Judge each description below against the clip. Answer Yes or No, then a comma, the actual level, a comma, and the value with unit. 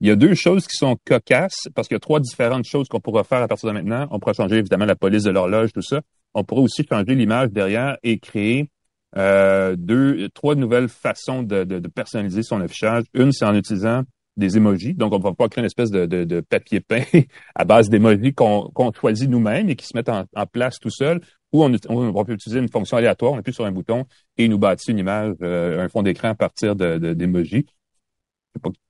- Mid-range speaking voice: No, low, 110 Hz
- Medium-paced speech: No, fast, 240 wpm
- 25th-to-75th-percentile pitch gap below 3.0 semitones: No, average, 4.1 semitones